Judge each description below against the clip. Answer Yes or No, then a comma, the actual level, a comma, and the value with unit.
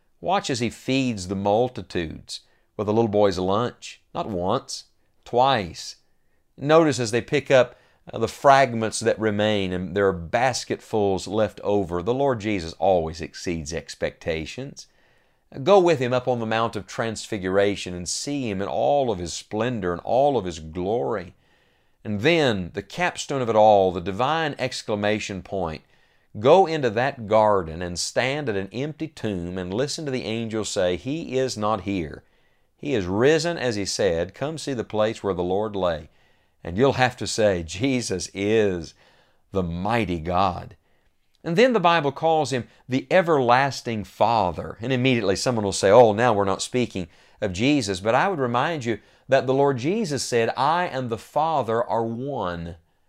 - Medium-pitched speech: No, low, 110 Hz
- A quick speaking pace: No, average, 170 wpm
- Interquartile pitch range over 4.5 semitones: Yes, average, 5.3 semitones